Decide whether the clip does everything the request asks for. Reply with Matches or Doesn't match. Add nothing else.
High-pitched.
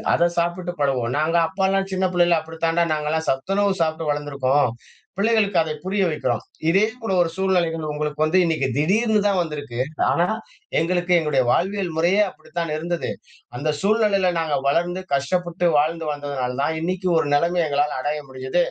Doesn't match